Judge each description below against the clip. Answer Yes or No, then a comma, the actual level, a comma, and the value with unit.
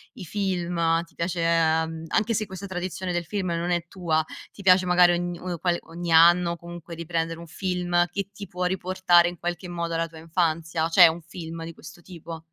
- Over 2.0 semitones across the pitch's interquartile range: No, narrow, 1.5 semitones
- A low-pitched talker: No, medium, 175 Hz